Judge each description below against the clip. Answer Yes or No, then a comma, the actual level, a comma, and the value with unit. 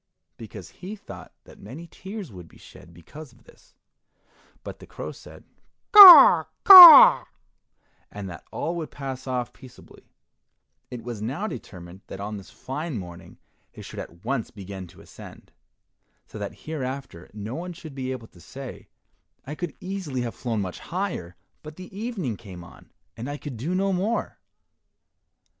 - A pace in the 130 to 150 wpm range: No, average, 160 wpm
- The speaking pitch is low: Yes, low, 130 Hz